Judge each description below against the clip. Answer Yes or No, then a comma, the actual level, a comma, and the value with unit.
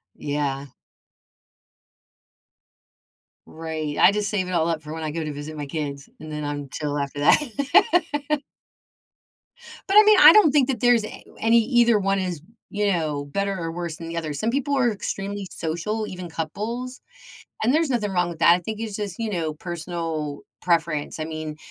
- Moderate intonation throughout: No, wide, 6.2 semitones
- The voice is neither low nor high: Yes, medium, 175 Hz